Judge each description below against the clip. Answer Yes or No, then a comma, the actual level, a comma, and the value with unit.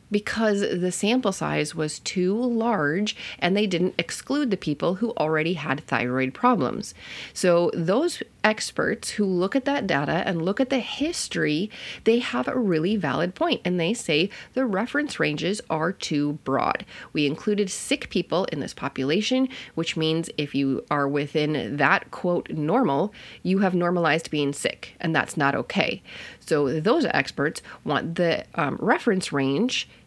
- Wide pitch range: Yes, wide, 6.4 semitones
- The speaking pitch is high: No, medium, 180 Hz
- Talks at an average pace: Yes, average, 160 wpm